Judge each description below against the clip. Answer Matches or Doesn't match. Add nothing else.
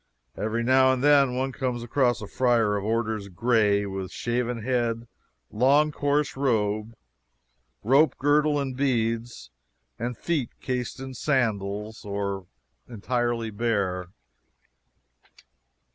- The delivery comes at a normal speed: Doesn't match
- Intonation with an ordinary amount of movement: Matches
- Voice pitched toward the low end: Matches